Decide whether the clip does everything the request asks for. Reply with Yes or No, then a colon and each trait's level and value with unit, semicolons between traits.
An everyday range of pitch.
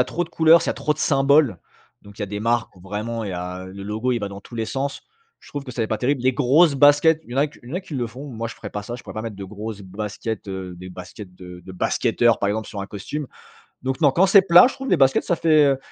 No: wide, 5.9 semitones